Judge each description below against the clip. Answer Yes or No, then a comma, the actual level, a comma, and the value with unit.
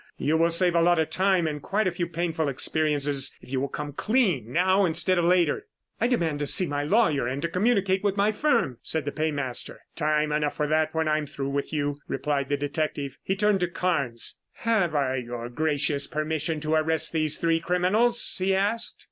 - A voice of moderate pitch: Yes, medium, 160 Hz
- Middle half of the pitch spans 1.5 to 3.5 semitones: No, average, 4.1 semitones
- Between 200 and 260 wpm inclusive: Yes, fast, 205 wpm